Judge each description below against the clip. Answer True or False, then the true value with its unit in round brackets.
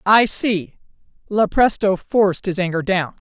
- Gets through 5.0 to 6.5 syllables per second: False (4.3 syllables/s)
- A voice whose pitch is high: True (195 Hz)